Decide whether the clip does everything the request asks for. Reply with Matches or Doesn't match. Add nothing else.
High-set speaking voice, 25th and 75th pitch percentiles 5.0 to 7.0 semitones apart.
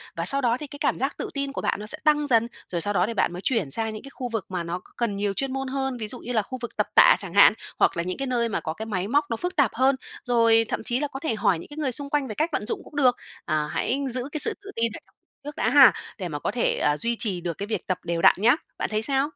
Matches